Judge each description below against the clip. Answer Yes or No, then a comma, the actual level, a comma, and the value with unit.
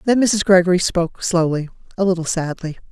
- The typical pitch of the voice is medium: Yes, medium, 180 Hz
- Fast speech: No, average, 165 wpm